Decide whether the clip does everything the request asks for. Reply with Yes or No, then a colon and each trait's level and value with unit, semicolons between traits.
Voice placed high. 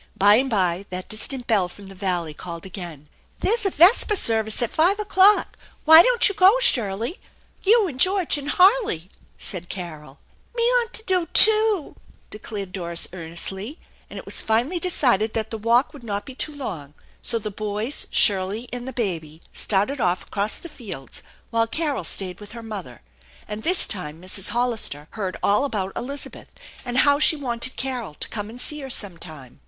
Yes: high, 225 Hz